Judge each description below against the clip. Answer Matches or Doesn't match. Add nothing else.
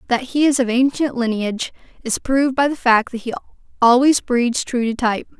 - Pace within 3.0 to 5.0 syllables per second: Doesn't match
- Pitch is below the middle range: Doesn't match